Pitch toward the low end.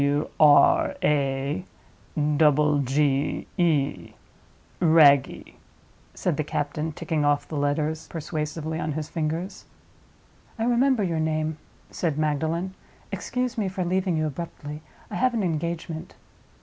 No: medium, 155 Hz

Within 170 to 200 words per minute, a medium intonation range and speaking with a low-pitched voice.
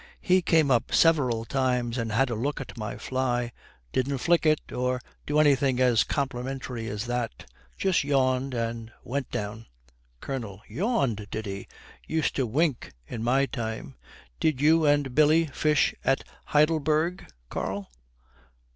No: average, 145 wpm; average, 4.2 semitones; low, 130 Hz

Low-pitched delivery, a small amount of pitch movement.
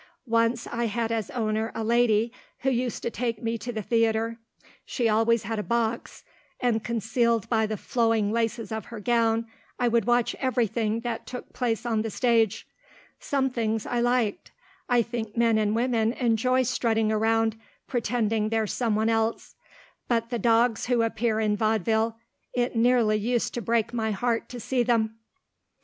No: high, 230 Hz; narrow, 1.4 semitones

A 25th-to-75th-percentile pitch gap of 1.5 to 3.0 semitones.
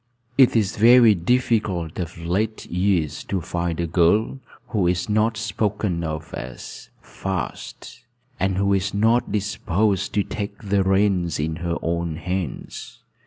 No: average, 3.7 semitones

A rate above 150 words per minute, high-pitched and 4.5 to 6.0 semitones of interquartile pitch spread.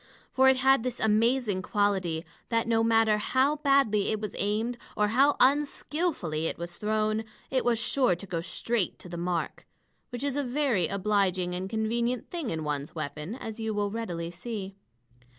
Yes: average, 175 wpm; high, 215 Hz; average, 5.1 semitones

